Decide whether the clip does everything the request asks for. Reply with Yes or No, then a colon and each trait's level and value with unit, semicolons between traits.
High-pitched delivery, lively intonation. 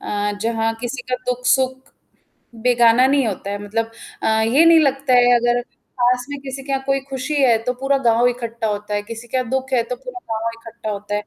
No: high, 245 Hz; narrow, 2.6 semitones